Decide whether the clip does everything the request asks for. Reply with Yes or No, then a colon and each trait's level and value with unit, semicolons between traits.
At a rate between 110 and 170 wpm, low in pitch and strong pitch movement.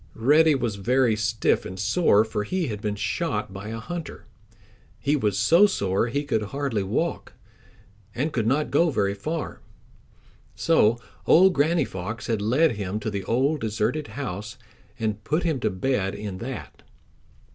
Yes: average, 160 wpm; low, 115 Hz; wide, 6.0 semitones